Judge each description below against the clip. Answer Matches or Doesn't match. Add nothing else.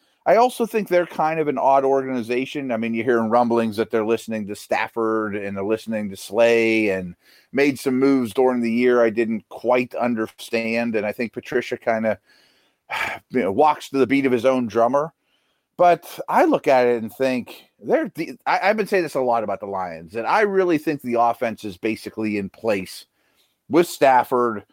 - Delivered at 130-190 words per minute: Doesn't match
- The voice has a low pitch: Matches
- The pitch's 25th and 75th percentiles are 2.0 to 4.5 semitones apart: Matches